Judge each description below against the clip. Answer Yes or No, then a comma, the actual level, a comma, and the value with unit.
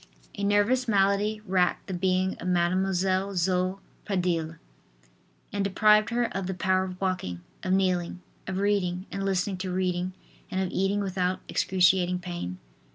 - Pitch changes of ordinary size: No, narrow, 1.4 semitones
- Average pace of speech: Yes, average, 150 wpm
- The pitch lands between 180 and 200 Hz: Yes, medium, 185 Hz